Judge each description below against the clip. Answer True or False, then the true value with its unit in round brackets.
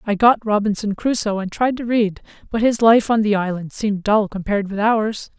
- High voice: True (215 Hz)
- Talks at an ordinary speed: False (210 wpm)